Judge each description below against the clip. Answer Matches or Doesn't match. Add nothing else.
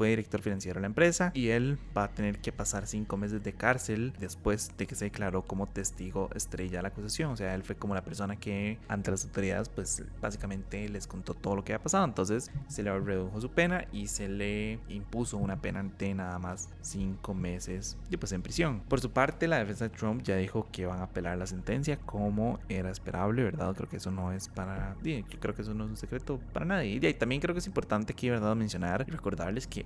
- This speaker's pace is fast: Matches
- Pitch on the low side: Matches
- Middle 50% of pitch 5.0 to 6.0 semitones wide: Doesn't match